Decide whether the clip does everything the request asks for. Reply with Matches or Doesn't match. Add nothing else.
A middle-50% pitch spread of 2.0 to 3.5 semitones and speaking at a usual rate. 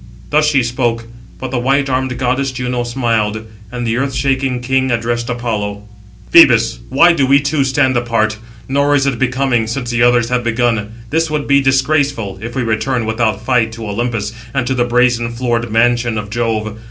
Matches